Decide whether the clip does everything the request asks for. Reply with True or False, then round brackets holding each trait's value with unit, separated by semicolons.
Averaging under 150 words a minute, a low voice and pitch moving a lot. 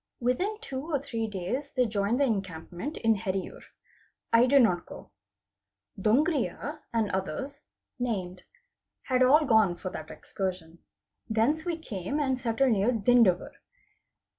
False (135 wpm; 230 Hz; 5.9 semitones)